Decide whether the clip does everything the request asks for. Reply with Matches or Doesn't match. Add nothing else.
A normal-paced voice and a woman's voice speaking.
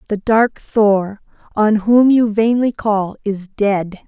Matches